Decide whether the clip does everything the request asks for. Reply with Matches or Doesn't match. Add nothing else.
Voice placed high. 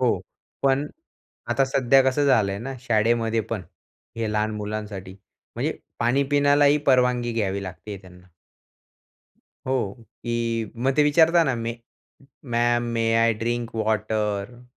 Doesn't match